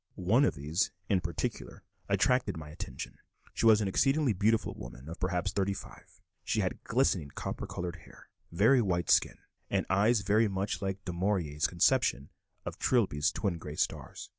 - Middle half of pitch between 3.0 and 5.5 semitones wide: Yes, average, 4.3 semitones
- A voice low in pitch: Yes, very low, 95 Hz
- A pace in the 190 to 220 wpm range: No, average, 165 wpm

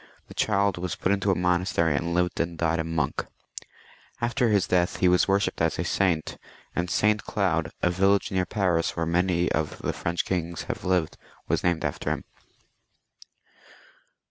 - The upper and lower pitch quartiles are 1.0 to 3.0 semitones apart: Yes, narrow, 2.6 semitones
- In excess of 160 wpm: Yes, average, 175 wpm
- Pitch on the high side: No, very low, 90 Hz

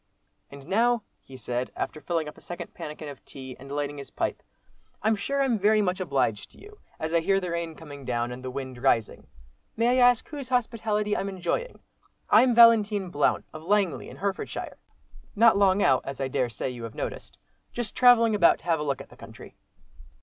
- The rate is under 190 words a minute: No, fast, 205 wpm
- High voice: No, medium, 175 Hz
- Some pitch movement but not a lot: No, wide, 7.9 semitones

